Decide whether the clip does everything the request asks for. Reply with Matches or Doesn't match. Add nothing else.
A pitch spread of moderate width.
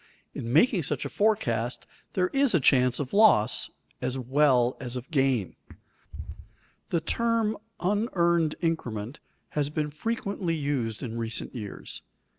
Doesn't match